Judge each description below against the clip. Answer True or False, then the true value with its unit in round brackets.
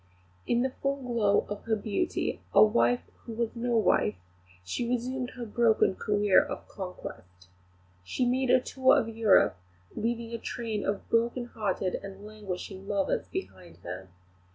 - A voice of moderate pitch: False (225 Hz)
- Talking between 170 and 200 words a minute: False (155 wpm)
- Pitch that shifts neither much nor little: True (3.4 semitones)